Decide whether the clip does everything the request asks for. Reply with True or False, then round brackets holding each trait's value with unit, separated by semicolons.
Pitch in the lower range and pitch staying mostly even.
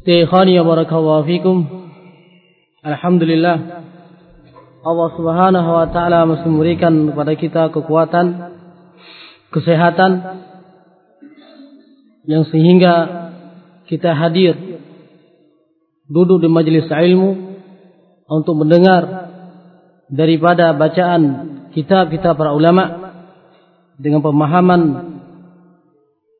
False (170 Hz; 1.9 semitones)